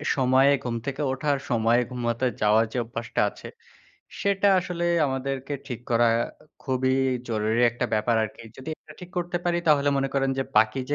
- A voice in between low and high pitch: No, low, 130 Hz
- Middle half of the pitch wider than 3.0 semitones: Yes, average, 3.4 semitones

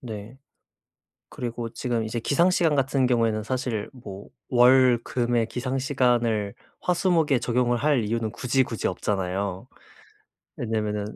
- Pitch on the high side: No, low, 120 Hz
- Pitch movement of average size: Yes, average, 3.1 semitones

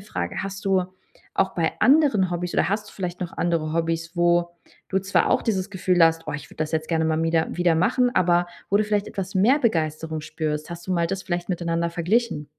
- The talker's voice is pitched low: No, medium, 175 Hz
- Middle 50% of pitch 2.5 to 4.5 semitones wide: Yes, average, 2.9 semitones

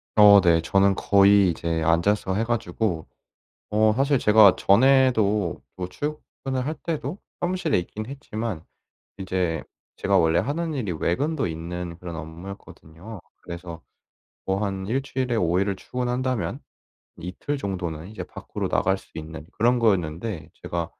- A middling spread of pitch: No, wide, 6.0 semitones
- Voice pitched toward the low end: Yes, low, 100 Hz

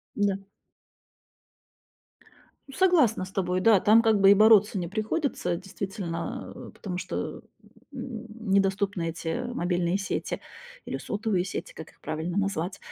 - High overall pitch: Yes, high, 195 Hz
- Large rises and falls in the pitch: No, average, 3.3 semitones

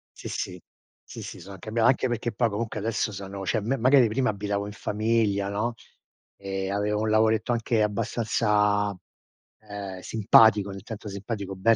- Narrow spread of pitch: Yes, narrow, 2.2 semitones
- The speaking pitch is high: No, low, 105 Hz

